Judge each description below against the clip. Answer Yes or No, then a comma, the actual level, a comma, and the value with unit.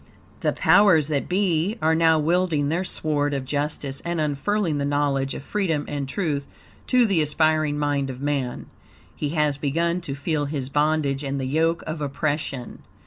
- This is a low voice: No, medium, 150 Hz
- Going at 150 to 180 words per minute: Yes, average, 170 wpm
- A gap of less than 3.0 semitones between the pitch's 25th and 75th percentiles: Yes, narrow, 2.6 semitones